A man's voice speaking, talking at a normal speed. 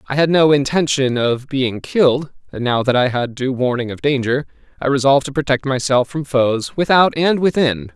Yes: male; average, 195 wpm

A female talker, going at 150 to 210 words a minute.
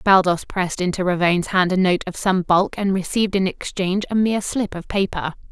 Yes: female; fast, 205 wpm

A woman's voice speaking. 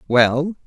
No: male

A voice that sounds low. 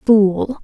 No: high, 215 Hz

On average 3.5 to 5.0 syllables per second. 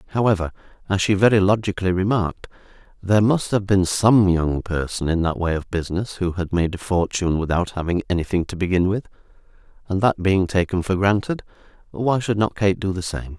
No: 5.8 syllables/s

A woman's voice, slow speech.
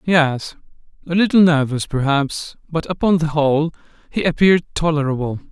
No: male; slow, 130 wpm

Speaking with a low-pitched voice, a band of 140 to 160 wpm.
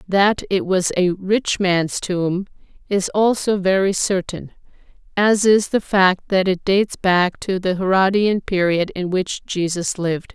No: high, 190 Hz; average, 155 wpm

